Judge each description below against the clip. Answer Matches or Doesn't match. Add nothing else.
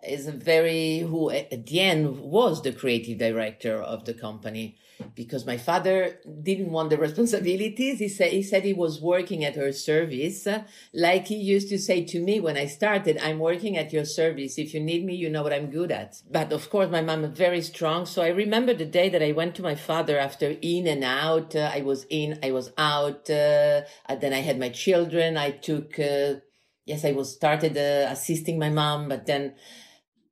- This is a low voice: Doesn't match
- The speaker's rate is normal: Doesn't match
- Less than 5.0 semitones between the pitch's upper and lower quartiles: Matches